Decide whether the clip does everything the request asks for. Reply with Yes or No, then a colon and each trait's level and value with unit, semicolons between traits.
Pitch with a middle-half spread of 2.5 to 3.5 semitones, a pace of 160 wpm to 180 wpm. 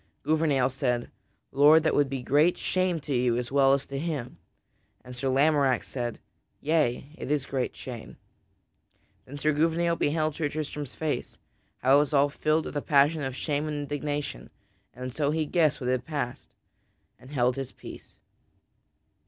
Yes: average, 2.9 semitones; average, 165 wpm